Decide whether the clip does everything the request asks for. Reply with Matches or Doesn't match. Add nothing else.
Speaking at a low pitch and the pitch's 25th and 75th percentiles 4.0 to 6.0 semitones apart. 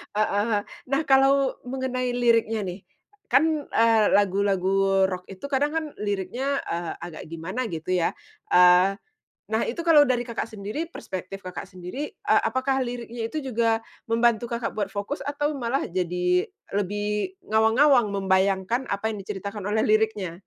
Doesn't match